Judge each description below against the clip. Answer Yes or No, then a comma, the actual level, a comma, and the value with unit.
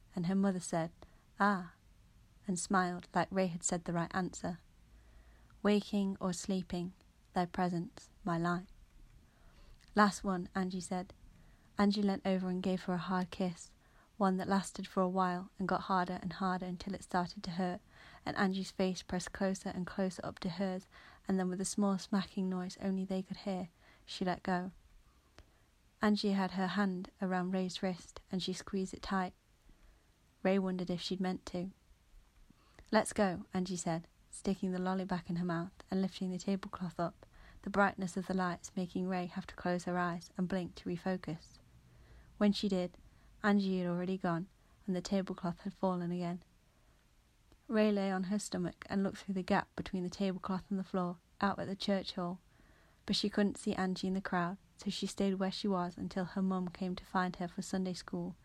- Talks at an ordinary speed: Yes, average, 185 wpm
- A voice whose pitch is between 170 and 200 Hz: Yes, medium, 185 Hz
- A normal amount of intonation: No, narrow, 1.5 semitones